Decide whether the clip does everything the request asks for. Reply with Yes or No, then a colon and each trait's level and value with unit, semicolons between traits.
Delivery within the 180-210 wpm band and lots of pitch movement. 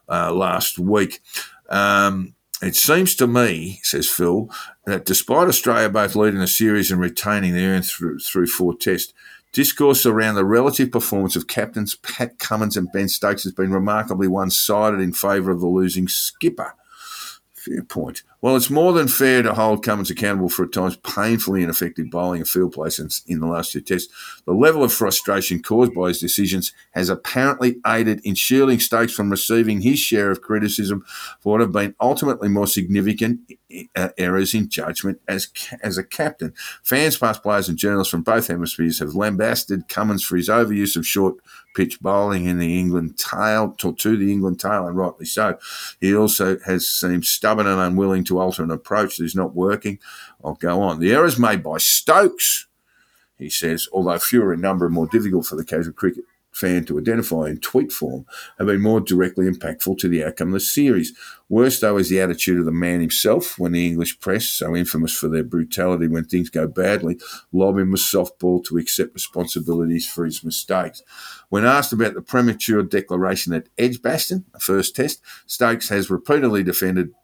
No: average, 185 wpm; average, 3.4 semitones